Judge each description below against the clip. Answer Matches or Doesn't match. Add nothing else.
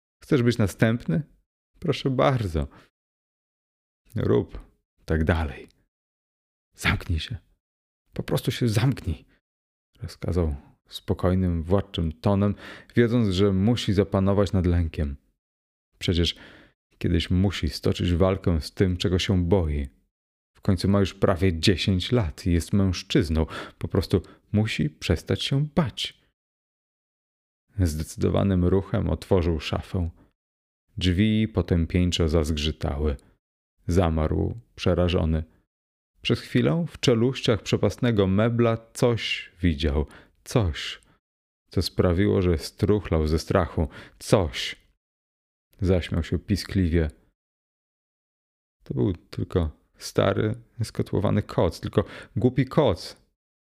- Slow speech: Matches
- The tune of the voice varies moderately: Matches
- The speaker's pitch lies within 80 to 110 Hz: Matches